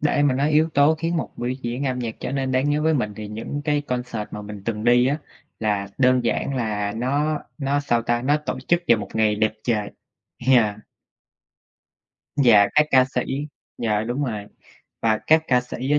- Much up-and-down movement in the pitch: No, average, 4.6 semitones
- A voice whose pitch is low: Yes, low, 125 Hz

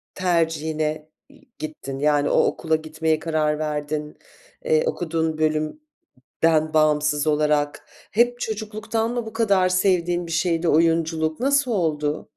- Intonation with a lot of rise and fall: No, average, 4.1 semitones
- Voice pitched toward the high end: No, medium, 160 Hz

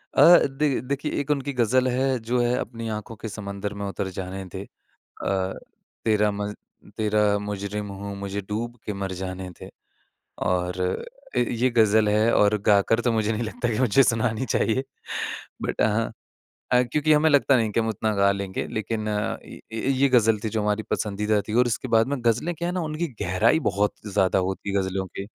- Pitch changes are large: No, average, 3.4 semitones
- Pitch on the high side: No, low, 110 Hz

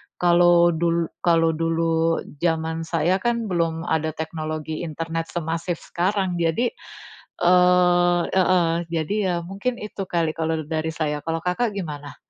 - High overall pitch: No, medium, 165 Hz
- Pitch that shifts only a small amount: Yes, narrow, 1.6 semitones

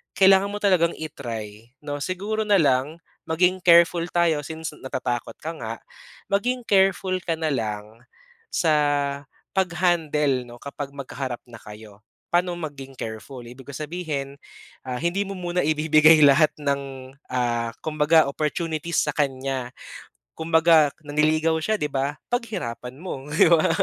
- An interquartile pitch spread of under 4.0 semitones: No, average, 4.5 semitones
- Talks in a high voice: No, medium, 155 Hz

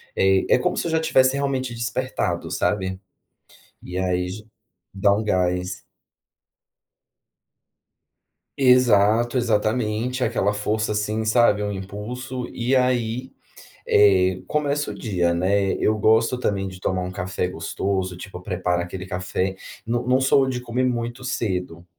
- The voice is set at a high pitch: No, low, 105 Hz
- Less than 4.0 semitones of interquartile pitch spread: No, average, 4.9 semitones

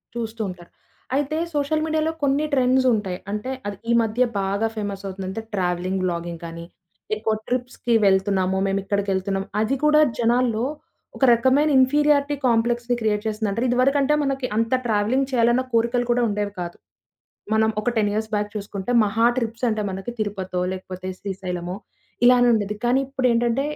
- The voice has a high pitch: Yes, high, 225 Hz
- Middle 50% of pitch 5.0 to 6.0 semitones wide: No, average, 4.3 semitones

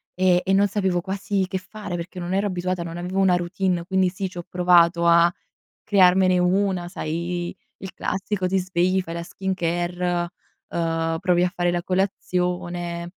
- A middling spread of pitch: No, narrow, 1.5 semitones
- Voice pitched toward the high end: No, medium, 180 Hz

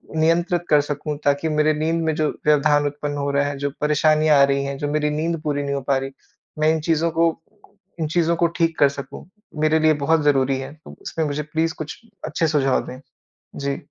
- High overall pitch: No, medium, 150 Hz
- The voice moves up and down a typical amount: No, narrow, 2.0 semitones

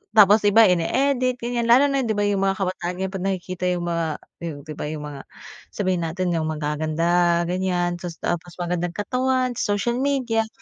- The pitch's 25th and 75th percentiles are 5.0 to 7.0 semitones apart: No, average, 4.6 semitones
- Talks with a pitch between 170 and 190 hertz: Yes, medium, 185 Hz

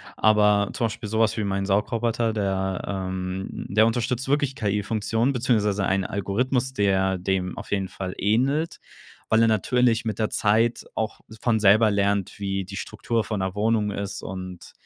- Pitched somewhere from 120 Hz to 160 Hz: No, low, 105 Hz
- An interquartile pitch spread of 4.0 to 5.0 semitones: No, average, 2.7 semitones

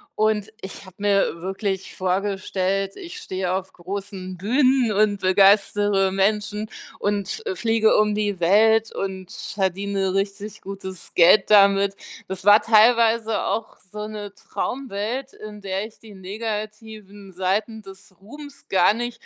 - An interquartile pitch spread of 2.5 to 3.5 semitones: No, narrow, 2.1 semitones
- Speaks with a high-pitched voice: Yes, high, 205 Hz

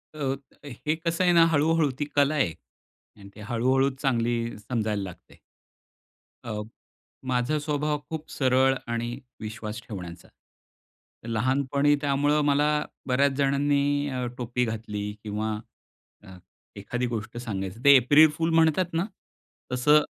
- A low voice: Yes, low, 130 Hz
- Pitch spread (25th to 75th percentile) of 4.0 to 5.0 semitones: Yes, average, 4.5 semitones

